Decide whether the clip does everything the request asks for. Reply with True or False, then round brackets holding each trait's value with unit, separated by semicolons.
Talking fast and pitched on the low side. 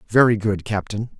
False (150 wpm; 110 Hz)